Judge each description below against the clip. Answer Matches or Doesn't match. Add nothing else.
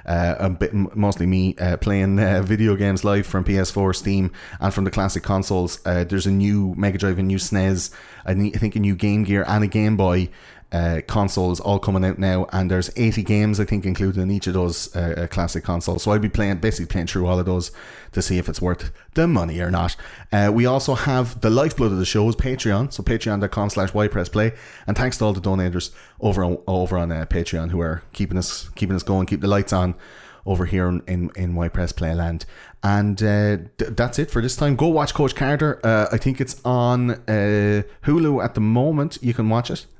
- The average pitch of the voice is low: Matches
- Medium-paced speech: Doesn't match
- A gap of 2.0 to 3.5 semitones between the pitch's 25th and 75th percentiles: Matches